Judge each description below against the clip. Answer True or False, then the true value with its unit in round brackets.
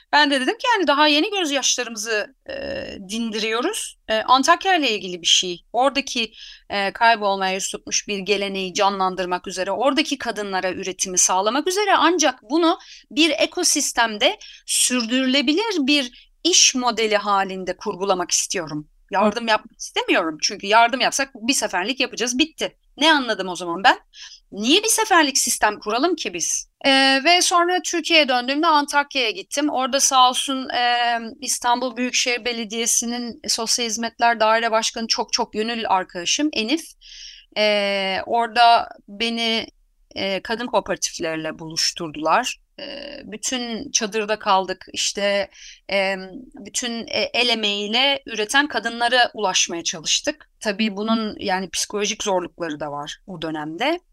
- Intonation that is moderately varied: False (5.9 semitones)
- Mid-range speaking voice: False (235 Hz)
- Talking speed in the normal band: True (130 wpm)